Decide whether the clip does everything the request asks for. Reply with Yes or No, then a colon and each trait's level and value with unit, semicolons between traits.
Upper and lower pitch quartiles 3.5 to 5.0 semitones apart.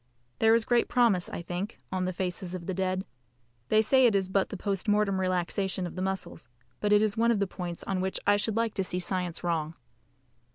No: narrow, 2.4 semitones